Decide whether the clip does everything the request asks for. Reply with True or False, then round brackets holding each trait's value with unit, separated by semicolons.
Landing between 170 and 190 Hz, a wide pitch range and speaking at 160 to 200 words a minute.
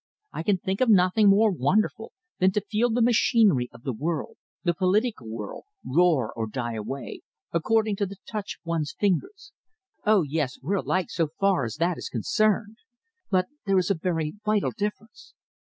True (185 Hz; 5.7 semitones; 175 wpm)